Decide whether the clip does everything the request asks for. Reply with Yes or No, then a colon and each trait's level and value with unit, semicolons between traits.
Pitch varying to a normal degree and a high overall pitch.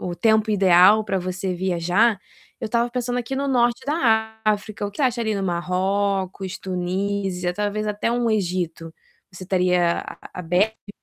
Yes: average, 3.4 semitones; high, 200 Hz